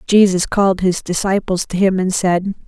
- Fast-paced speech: No, average, 180 wpm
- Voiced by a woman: Yes, female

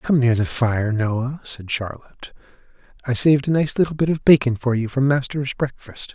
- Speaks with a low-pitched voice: Yes, low, 130 Hz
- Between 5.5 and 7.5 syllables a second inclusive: No, 5.1 syllables/s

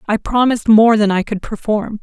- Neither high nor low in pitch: No, high, 215 Hz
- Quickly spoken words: Yes, fast, 210 wpm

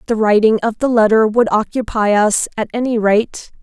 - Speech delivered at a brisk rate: No, average, 180 wpm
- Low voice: No, high, 220 Hz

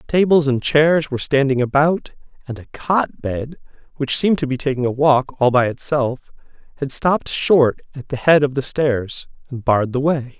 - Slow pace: No, average, 190 wpm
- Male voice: Yes, male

